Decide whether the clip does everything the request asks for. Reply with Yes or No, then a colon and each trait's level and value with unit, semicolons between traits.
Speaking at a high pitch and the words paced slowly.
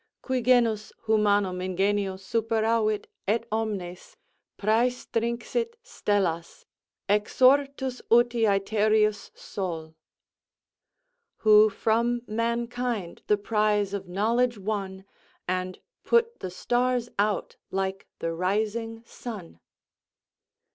Yes: high, 215 Hz; slow, 85 wpm